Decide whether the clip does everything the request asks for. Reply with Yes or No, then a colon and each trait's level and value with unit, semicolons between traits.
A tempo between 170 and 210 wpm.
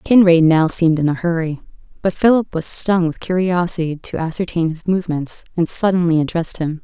Yes: average, 175 wpm